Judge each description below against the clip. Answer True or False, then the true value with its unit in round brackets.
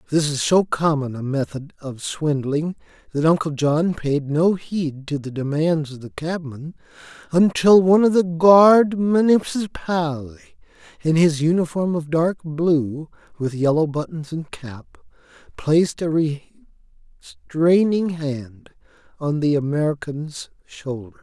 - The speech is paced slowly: True (125 wpm)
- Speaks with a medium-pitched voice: True (155 Hz)